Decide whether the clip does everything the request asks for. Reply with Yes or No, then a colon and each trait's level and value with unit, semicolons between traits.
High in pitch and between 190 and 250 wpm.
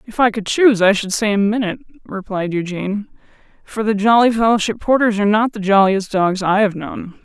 Yes: high, 210 Hz; average, 200 wpm